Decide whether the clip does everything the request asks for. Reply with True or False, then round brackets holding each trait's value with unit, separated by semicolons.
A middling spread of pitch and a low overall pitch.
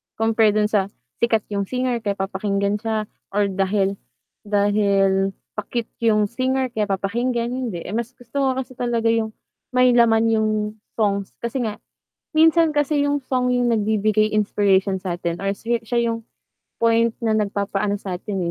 False (3.0 semitones; 220 Hz)